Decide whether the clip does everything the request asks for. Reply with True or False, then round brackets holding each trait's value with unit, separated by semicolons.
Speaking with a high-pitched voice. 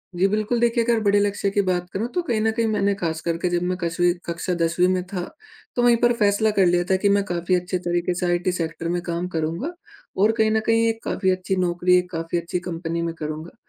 False (180 Hz)